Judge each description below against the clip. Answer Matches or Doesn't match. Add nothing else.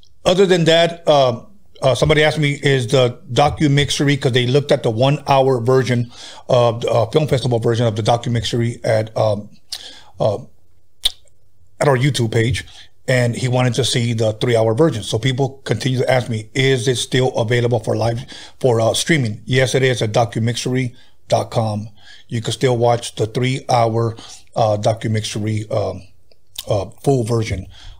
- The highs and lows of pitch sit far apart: Doesn't match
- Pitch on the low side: Matches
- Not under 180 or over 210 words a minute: Doesn't match